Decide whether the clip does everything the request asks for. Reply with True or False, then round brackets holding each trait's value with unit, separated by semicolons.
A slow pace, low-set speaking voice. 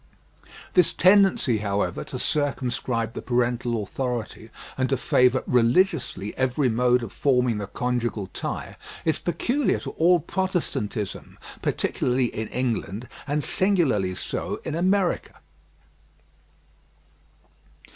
True (105 wpm; 125 Hz)